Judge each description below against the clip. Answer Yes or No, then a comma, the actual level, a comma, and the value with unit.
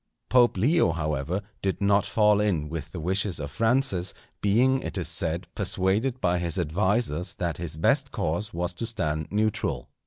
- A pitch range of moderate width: Yes, average, 4.6 semitones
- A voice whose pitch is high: No, very low, 95 Hz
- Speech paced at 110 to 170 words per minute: Yes, average, 165 wpm